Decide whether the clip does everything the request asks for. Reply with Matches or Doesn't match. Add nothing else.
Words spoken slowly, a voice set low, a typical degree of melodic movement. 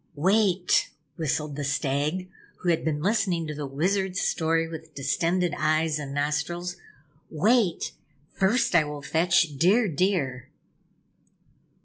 Doesn't match